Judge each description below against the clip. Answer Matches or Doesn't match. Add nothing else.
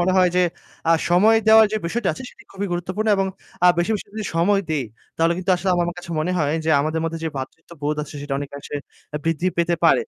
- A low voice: Doesn't match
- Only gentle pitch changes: Doesn't match